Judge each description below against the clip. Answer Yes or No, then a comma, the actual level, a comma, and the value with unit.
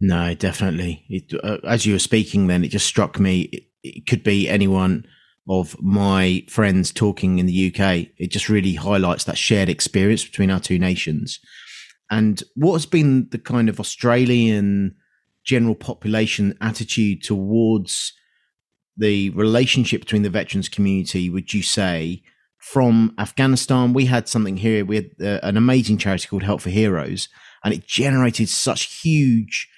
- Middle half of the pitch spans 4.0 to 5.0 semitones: No, average, 3.1 semitones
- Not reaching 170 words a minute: Yes, average, 155 wpm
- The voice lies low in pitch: Yes, low, 105 Hz